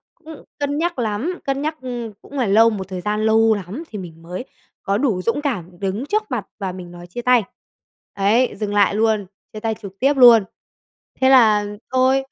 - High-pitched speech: Yes, high, 220 Hz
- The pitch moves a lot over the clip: No, average, 4.6 semitones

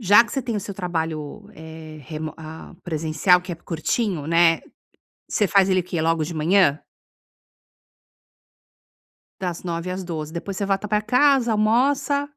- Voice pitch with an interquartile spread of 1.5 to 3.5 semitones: No, average, 4.6 semitones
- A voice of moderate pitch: Yes, medium, 180 Hz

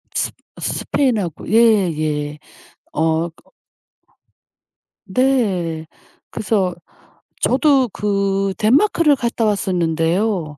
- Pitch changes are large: Yes, wide, 5.9 semitones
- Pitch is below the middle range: No, high, 195 Hz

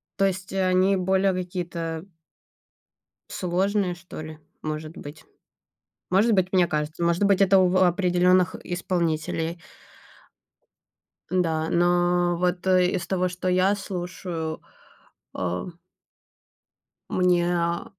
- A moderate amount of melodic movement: No, narrow, 1.6 semitones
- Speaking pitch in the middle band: Yes, medium, 180 Hz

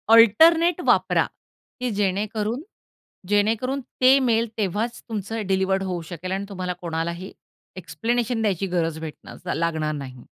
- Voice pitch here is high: Yes, high, 200 Hz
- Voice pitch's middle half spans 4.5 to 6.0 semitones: Yes, average, 4.8 semitones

